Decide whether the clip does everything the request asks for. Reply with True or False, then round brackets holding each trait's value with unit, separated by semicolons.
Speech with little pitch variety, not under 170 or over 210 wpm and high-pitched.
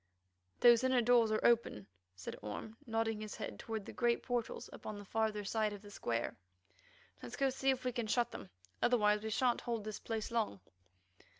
True (2.3 semitones; 190 wpm; 225 Hz)